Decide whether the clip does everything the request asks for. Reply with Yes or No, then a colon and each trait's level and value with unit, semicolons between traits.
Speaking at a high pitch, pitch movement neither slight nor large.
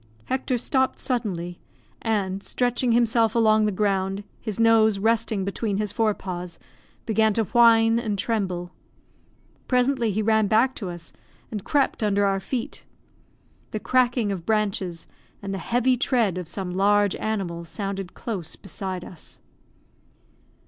Yes: high, 215 Hz; average, 3.1 semitones